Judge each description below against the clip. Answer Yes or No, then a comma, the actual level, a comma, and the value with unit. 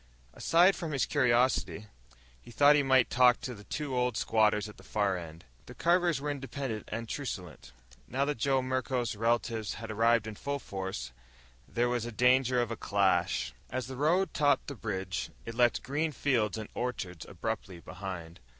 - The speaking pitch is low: Yes, low, 120 Hz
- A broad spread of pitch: No, average, 4.4 semitones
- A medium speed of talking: Yes, average, 175 wpm